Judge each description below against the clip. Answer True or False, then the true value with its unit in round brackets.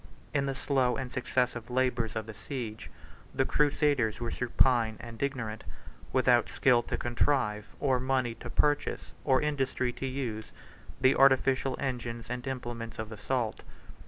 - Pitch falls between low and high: False (125 Hz)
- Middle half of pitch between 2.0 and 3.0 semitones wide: True (2.5 semitones)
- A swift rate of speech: False (145 wpm)